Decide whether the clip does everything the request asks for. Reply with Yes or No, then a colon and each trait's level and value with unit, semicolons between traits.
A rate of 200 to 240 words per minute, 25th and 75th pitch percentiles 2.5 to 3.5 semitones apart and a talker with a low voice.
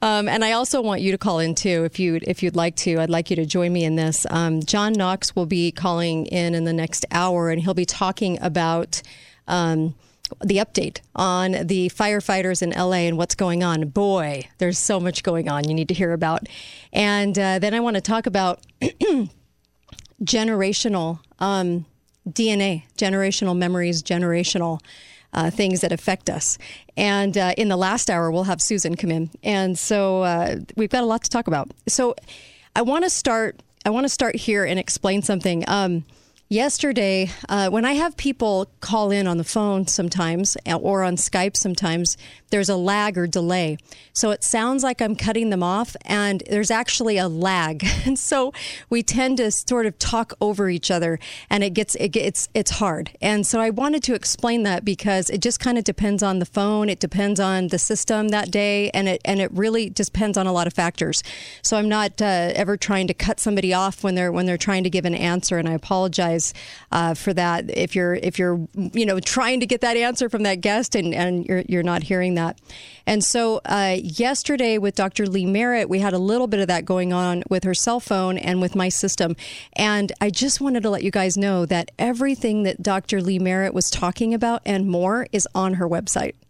No: fast, 205 wpm; average, 3.2 semitones; high, 190 Hz